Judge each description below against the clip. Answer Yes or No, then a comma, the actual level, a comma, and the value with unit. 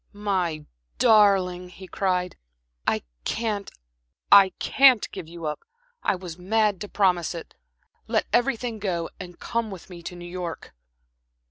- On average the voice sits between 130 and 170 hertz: No, medium, 185 Hz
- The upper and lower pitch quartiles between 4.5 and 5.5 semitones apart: No, average, 3.1 semitones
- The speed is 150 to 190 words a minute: No, average, 140 wpm